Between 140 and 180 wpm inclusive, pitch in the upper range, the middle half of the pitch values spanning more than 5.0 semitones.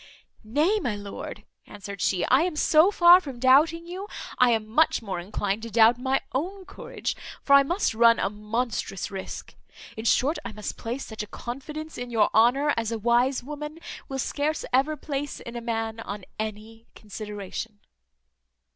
Yes: average, 175 wpm; high, 240 Hz; wide, 5.5 semitones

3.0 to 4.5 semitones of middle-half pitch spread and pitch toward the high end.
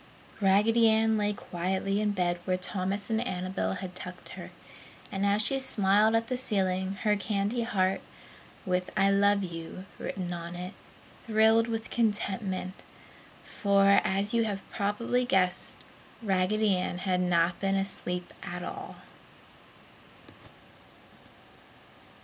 No: narrow, 2.6 semitones; high, 195 Hz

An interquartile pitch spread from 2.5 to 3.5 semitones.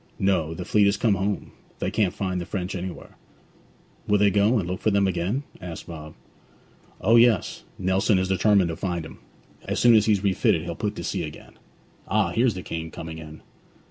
Yes: average, 3.2 semitones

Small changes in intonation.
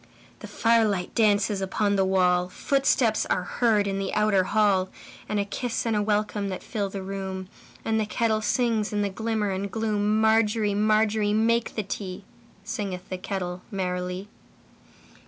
Yes: narrow, 2.3 semitones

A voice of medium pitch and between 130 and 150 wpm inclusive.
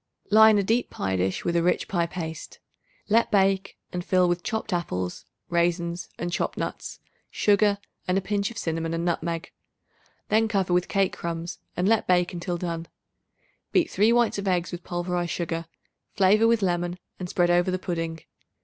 No: medium, 180 Hz; average, 175 wpm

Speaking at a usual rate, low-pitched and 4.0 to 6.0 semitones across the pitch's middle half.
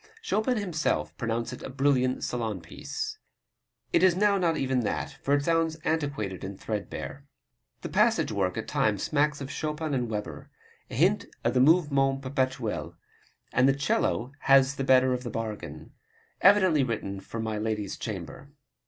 Yes: average, 160 wpm; low, 130 Hz; average, 5.1 semitones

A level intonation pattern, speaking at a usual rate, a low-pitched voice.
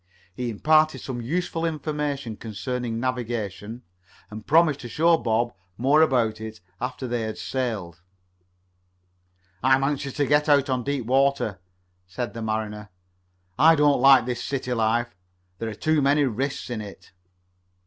No: average, 4.2 semitones; average, 145 wpm; low, 125 Hz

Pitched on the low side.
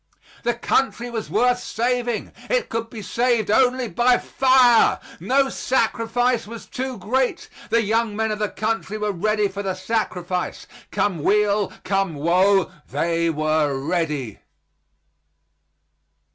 No: high, 215 Hz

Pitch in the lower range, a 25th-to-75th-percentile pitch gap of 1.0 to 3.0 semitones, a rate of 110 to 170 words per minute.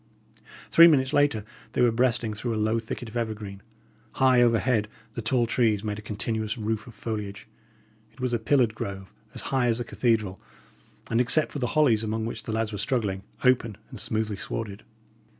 No: low, 115 Hz; narrow, 2.4 semitones; average, 185 wpm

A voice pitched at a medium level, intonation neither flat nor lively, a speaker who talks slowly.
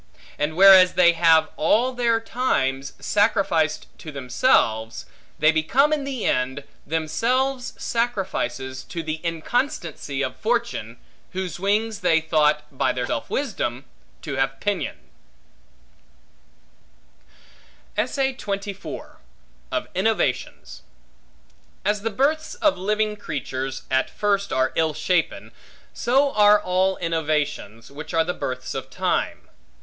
No: medium, 175 Hz; wide, 7.2 semitones; slow, 115 wpm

